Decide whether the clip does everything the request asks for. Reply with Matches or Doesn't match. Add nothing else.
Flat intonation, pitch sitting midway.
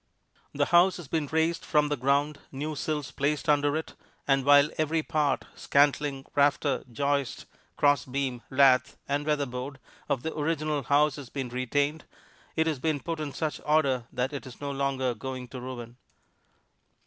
Matches